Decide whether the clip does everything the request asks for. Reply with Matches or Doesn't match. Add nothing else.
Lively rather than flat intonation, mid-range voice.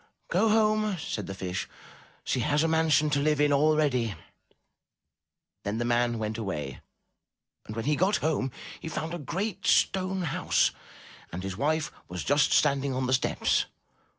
Matches